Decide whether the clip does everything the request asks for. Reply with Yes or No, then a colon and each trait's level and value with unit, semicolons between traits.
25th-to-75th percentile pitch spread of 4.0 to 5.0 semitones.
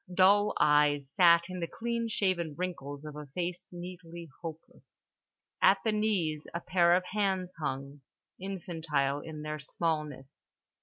No: average, 3.6 semitones